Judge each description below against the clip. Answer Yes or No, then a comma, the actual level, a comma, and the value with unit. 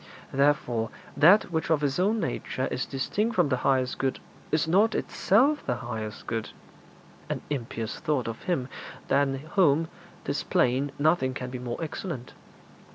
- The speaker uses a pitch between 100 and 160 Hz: Yes, medium, 140 Hz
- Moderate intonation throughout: Yes, average, 4.9 semitones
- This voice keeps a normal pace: Yes, average, 155 wpm